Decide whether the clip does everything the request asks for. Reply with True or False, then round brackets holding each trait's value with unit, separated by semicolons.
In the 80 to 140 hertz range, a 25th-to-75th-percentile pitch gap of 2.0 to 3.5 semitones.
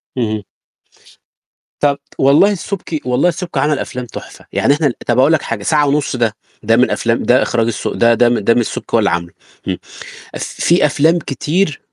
False (135 Hz; 4.5 semitones)